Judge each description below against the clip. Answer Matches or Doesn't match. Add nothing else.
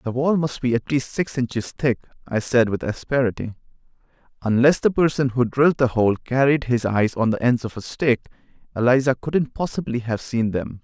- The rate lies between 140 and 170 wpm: Doesn't match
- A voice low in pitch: Matches